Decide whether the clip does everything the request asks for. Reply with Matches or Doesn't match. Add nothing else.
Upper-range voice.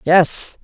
Doesn't match